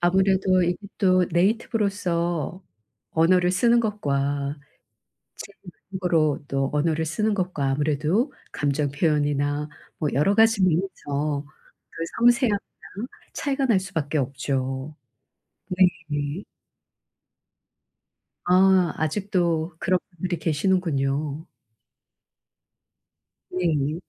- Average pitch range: Yes, average, 4.4 semitones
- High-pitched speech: No, medium, 170 Hz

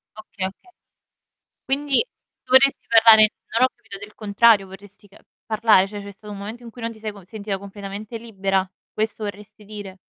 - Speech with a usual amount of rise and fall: No, narrow, 2.2 semitones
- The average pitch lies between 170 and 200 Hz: No, high, 210 Hz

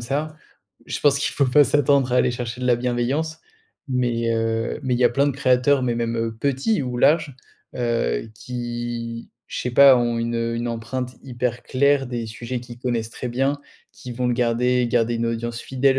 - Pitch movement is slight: Yes, narrow, 2.1 semitones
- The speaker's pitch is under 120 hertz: No, low, 125 Hz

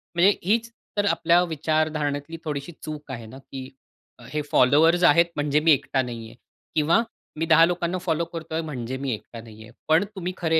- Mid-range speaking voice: Yes, medium, 155 Hz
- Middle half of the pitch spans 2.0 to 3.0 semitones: No, average, 3.6 semitones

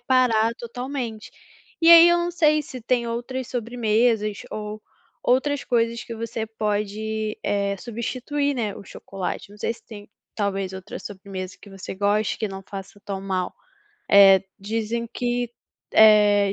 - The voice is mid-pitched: No, high, 220 Hz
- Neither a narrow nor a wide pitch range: Yes, average, 3.2 semitones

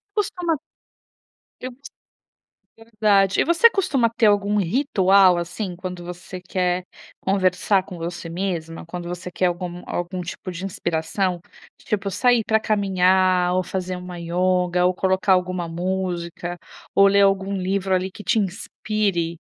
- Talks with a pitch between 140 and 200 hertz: Yes, medium, 185 Hz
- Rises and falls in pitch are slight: Yes, narrow, 2.1 semitones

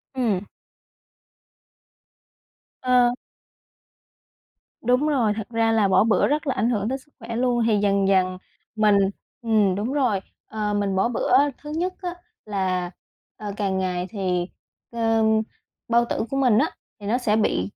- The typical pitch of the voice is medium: No, high, 220 Hz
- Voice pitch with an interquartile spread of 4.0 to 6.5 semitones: No, average, 3.6 semitones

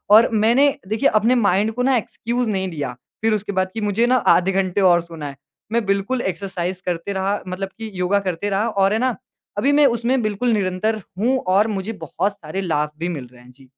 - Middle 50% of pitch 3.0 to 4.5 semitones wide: Yes, average, 3.6 semitones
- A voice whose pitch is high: Yes, high, 200 Hz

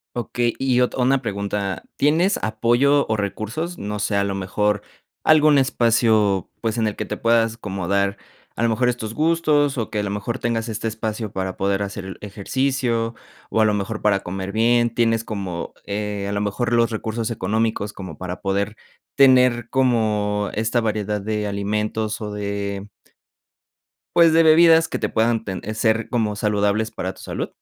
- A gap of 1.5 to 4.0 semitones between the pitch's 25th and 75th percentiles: Yes, average, 2.8 semitones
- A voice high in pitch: No, low, 110 Hz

